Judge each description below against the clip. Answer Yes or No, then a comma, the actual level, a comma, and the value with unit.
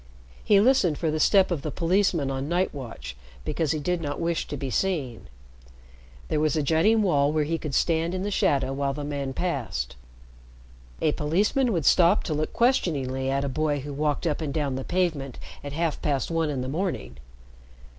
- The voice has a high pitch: No, medium, 155 Hz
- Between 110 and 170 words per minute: No, average, 195 wpm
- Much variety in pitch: No, average, 3.9 semitones